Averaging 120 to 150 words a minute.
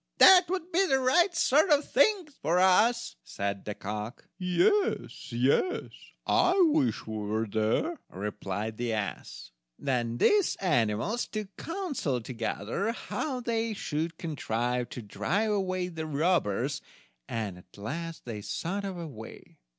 Yes: average, 140 wpm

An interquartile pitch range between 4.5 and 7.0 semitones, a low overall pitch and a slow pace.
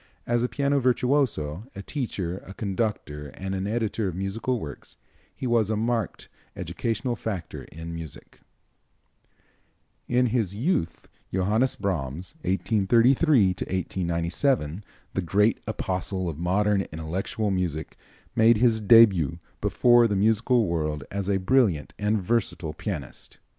Yes: average, 4.8 semitones; low, 100 Hz; slow, 125 wpm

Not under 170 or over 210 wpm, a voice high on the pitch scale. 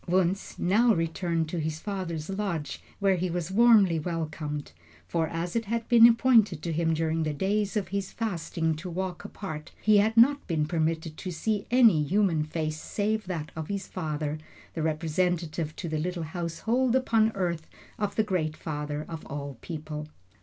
No: average, 175 wpm; medium, 170 Hz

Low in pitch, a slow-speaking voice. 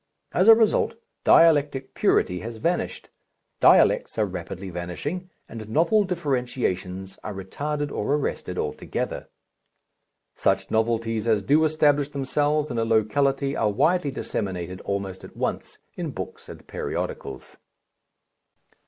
Yes: low, 125 Hz; slow, 120 wpm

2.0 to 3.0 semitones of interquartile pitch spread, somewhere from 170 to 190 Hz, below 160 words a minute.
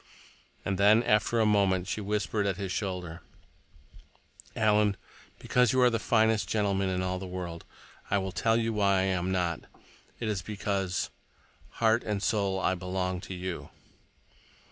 No: narrow, 2.5 semitones; low, 100 Hz; average, 150 wpm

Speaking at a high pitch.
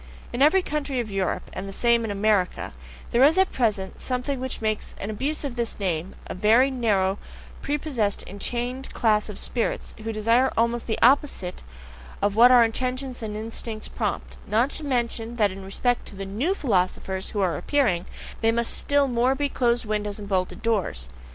Yes: high, 230 Hz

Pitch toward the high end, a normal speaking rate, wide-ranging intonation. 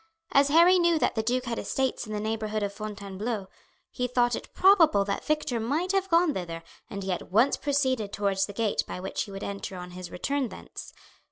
No: high, 225 Hz; fast, 210 wpm; wide, 6.0 semitones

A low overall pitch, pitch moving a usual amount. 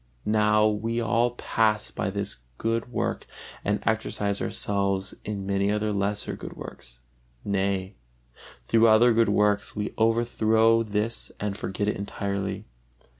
No: low, 105 Hz; narrow, 2.0 semitones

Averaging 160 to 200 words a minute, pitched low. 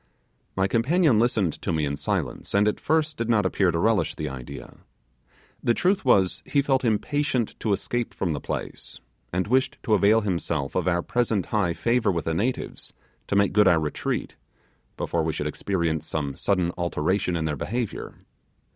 Yes: average, 180 wpm; low, 100 Hz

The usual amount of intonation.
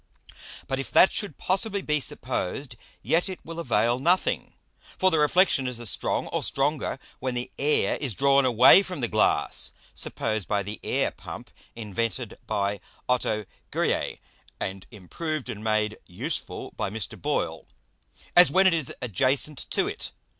No: wide, 6.4 semitones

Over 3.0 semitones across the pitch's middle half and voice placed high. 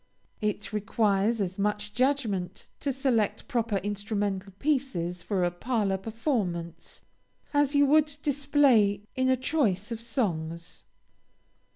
Yes: average, 5.2 semitones; high, 215 Hz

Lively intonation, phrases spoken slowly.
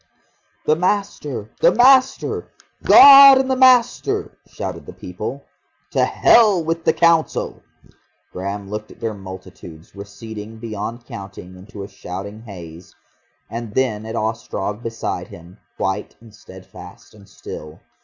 Yes: wide, 8.9 semitones; slow, 130 wpm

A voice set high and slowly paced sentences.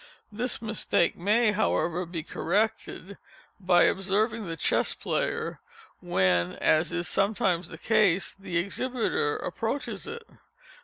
Yes: high, 195 Hz; slow, 115 wpm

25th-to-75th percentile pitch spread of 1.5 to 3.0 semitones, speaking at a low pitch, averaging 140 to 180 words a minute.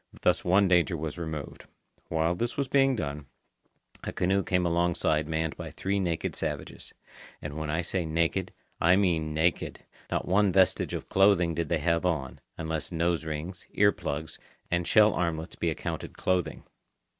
Yes: average, 2.7 semitones; very low, 85 Hz; average, 165 wpm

